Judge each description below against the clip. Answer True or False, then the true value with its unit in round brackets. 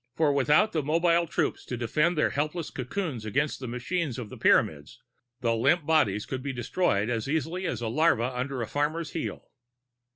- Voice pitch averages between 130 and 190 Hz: True (140 Hz)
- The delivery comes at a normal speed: True (185 wpm)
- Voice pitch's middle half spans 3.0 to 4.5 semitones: False (5.2 semitones)